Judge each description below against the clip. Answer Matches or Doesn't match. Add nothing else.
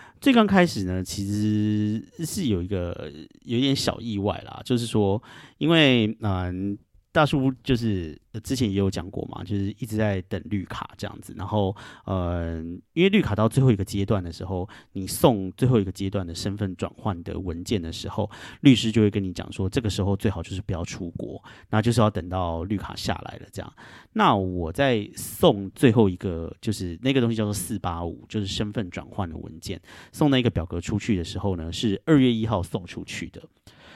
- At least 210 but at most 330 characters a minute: Matches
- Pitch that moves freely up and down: Doesn't match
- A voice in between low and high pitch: Doesn't match